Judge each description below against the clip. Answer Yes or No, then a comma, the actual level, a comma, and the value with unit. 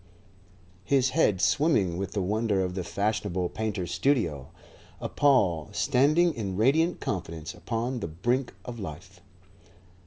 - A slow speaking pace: Yes, slow, 130 wpm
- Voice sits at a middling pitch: No, low, 105 Hz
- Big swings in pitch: Yes, wide, 6.0 semitones